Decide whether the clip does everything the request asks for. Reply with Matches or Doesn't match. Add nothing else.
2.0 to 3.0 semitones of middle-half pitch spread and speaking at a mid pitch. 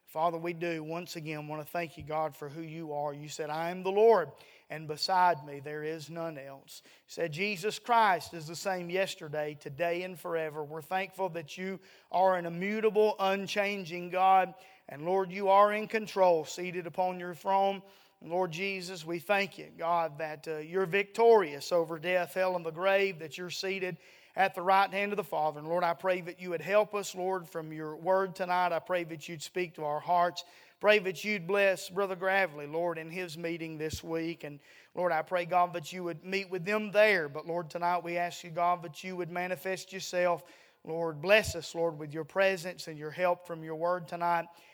Matches